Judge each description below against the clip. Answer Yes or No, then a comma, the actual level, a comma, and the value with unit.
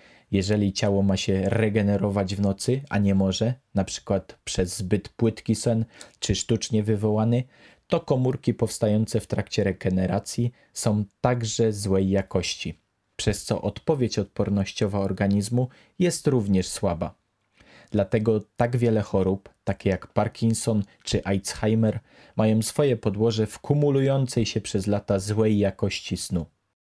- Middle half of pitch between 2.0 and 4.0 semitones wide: Yes, average, 2.7 semitones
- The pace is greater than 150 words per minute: No, average, 125 wpm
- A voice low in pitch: Yes, low, 105 Hz